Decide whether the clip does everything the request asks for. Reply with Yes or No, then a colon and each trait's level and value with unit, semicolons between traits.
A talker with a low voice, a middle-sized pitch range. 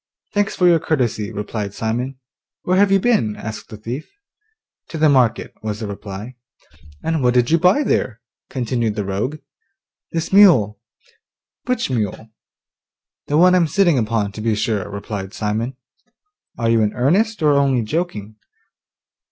No: low, 120 Hz; wide, 7.1 semitones